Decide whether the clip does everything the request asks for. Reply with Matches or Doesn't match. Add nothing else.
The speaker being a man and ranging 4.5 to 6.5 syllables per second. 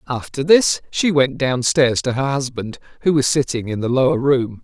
Matches